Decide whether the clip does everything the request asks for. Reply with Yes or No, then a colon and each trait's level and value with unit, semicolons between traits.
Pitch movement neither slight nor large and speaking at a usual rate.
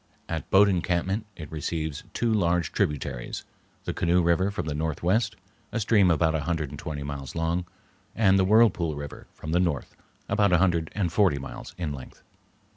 Yes: average, 3.8 semitones; average, 180 wpm